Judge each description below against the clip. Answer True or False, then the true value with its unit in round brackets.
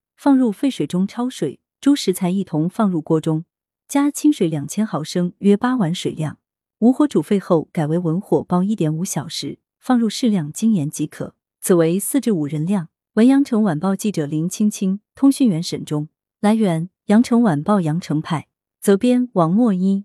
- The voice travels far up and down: True (5.7 semitones)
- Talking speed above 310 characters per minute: False (260 characters per minute)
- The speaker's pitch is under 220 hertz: True (190 Hz)